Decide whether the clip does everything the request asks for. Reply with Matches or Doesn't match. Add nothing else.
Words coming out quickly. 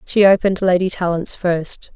Doesn't match